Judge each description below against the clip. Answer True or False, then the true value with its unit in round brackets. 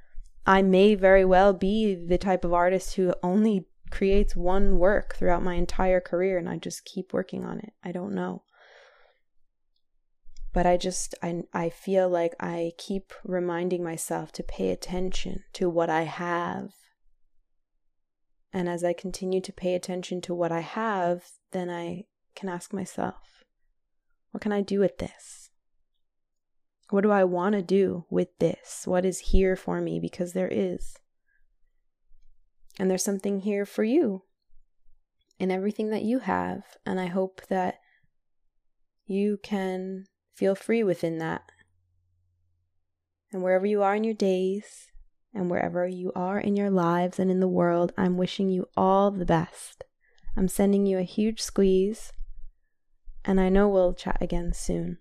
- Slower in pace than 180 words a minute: True (155 wpm)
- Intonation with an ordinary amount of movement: False (2.1 semitones)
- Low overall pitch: False (185 Hz)